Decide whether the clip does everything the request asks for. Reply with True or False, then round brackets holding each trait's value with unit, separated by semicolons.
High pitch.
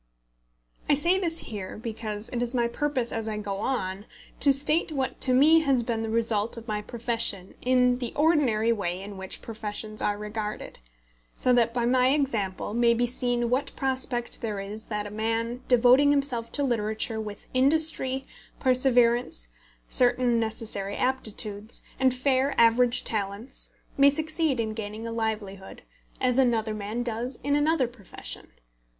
True (235 Hz)